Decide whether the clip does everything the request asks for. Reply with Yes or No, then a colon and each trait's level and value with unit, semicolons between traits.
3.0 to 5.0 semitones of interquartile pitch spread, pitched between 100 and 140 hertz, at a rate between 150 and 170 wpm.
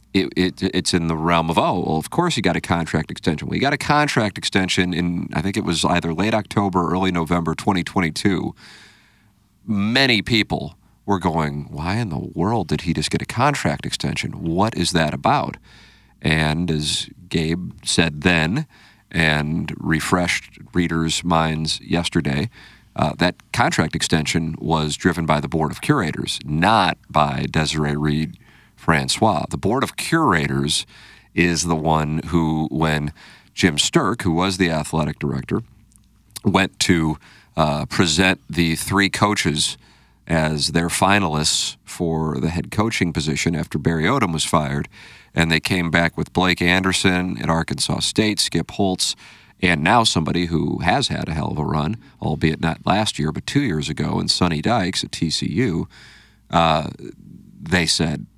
No: average, 3.4 semitones; very low, 85 Hz; average, 160 wpm